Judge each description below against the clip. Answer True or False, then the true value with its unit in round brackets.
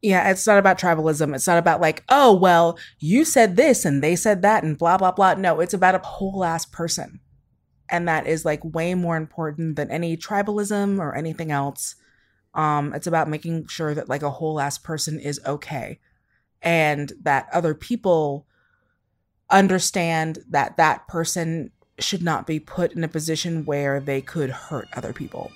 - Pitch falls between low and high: True (165 Hz)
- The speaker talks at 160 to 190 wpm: True (180 wpm)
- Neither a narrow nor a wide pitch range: True (3.1 semitones)